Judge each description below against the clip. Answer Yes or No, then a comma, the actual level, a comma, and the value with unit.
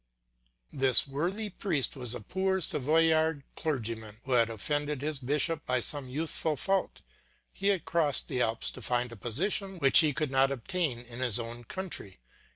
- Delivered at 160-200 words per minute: Yes, average, 165 wpm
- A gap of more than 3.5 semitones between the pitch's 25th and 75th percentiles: Yes, average, 5.0 semitones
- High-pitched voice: No, medium, 140 Hz